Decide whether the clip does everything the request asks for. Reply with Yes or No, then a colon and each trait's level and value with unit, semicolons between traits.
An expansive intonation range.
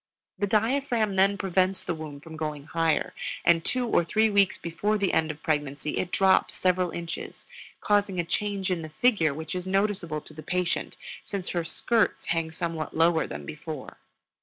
No: average, 3.9 semitones